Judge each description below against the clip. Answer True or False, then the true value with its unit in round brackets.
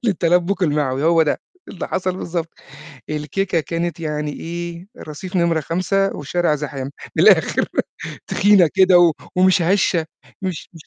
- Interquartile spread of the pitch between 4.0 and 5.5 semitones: False (3.1 semitones)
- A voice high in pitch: False (170 Hz)